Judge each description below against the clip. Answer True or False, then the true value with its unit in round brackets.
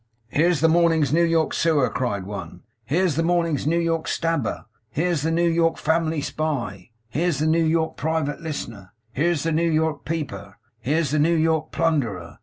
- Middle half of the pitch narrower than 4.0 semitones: True (2.8 semitones)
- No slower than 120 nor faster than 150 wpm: False (175 wpm)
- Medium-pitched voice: True (160 Hz)